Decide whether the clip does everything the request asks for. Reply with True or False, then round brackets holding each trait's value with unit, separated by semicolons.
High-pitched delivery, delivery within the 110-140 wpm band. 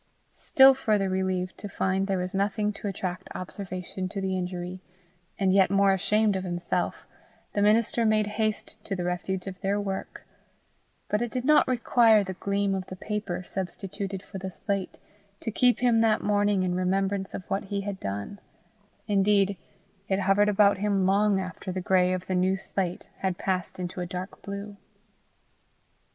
False (195 Hz; 170 wpm)